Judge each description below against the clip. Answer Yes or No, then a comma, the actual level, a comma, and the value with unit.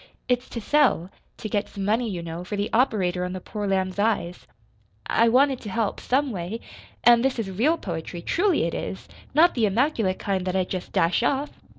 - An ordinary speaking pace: No, fast, 210 wpm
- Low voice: No, high, 210 Hz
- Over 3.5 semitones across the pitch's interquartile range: Yes, average, 5.0 semitones